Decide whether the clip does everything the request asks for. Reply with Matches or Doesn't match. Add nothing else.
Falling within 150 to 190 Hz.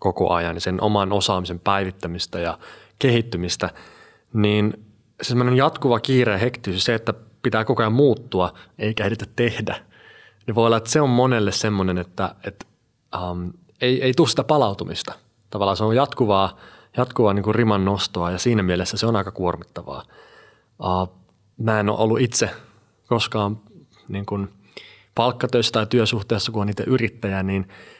Doesn't match